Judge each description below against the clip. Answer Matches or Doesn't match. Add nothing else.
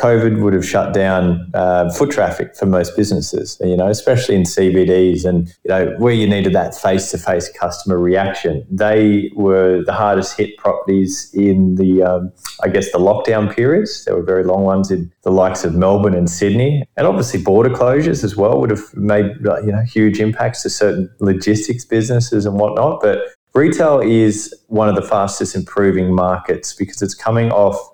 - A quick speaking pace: Doesn't match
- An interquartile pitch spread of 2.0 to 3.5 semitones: Matches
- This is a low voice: Matches